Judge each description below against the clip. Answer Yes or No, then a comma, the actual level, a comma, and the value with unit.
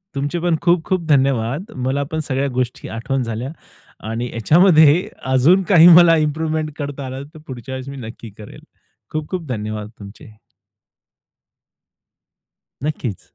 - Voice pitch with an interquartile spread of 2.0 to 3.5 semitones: No, average, 4.4 semitones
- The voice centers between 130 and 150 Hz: Yes, medium, 140 Hz